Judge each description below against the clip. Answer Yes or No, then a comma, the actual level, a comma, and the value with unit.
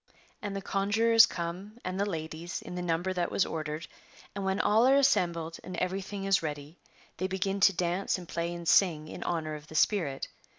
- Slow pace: No, average, 200 wpm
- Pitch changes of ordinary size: Yes, average, 3.1 semitones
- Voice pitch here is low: No, medium, 180 Hz